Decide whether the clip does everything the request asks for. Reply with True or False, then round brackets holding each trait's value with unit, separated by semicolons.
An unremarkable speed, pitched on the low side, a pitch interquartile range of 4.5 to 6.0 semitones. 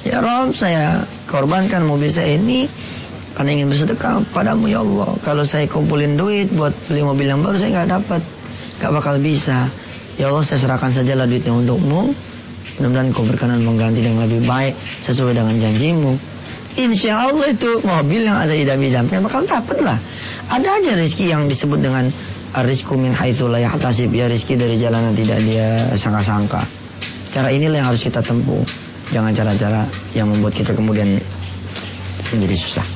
True (155 wpm; 130 Hz; 5.4 semitones)